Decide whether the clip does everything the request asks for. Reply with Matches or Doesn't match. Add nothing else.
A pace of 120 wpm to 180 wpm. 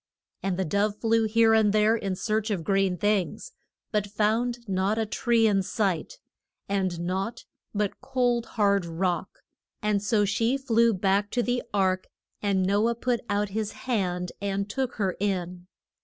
Matches